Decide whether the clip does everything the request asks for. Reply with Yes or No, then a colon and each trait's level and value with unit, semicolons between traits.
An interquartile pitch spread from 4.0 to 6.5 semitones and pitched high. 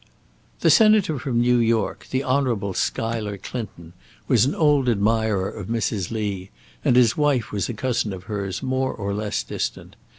No: average, 4.3 semitones; low, 115 Hz